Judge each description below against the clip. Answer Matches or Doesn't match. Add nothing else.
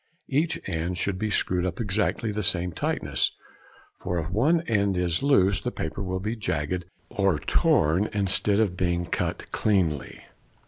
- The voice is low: Matches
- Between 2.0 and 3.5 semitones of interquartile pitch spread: Matches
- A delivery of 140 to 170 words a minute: Matches